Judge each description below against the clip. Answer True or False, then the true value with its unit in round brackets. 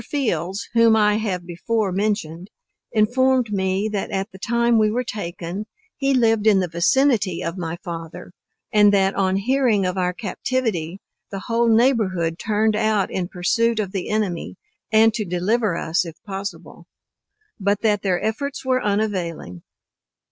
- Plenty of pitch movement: False (3.8 semitones)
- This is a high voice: True (205 Hz)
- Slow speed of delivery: False (155 wpm)